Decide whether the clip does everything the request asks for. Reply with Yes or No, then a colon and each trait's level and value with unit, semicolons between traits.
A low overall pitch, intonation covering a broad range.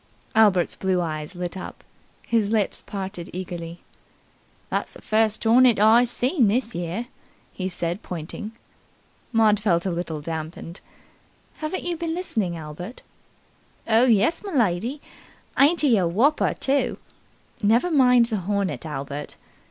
No: high, 210 Hz; wide, 5.7 semitones